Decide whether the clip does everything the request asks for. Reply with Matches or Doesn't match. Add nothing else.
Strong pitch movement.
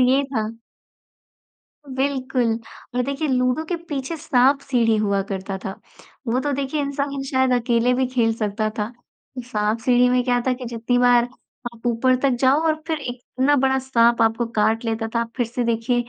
Doesn't match